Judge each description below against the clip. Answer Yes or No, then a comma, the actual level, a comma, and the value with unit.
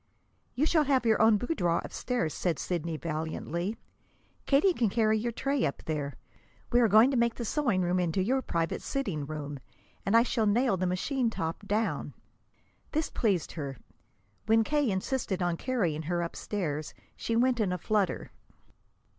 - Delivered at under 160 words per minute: No, average, 165 wpm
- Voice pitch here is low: No, high, 210 Hz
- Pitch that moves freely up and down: Yes, wide, 6.2 semitones